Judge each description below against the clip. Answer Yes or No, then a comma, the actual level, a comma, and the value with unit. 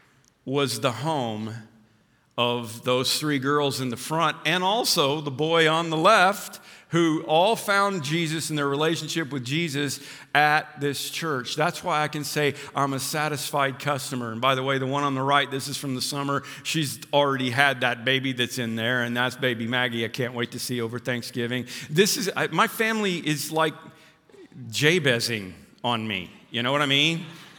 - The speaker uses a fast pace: No, average, 185 wpm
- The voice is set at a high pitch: No, medium, 140 Hz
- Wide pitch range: No, average, 3.6 semitones